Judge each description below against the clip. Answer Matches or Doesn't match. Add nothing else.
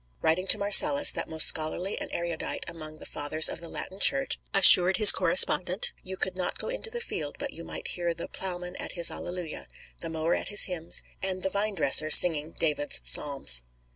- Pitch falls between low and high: Matches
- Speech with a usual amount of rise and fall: Matches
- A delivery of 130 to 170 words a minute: Doesn't match